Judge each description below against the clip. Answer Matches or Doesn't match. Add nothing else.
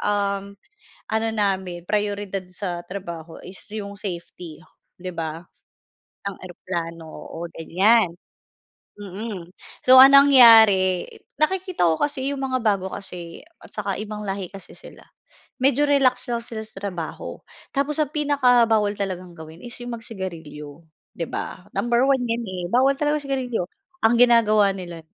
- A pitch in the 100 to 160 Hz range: Doesn't match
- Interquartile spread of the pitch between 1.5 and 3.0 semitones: Doesn't match